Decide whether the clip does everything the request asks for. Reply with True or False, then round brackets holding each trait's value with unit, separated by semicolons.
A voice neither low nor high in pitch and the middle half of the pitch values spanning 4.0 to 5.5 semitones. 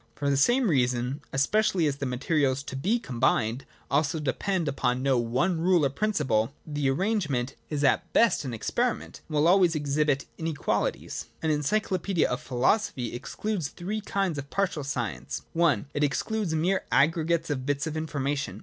True (150 Hz; 4.9 semitones)